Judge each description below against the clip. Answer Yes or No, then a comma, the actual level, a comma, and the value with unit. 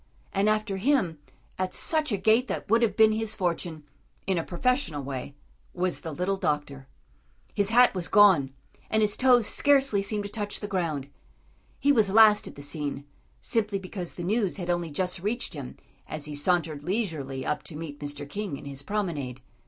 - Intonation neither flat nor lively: No, wide, 6.2 semitones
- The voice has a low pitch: No, medium, 185 Hz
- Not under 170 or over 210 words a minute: Yes, average, 185 wpm